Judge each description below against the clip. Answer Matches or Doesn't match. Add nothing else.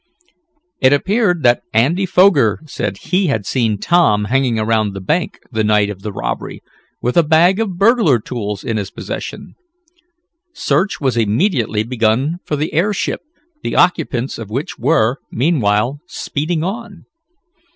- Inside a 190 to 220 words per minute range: Doesn't match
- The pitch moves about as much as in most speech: Doesn't match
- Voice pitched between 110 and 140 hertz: Matches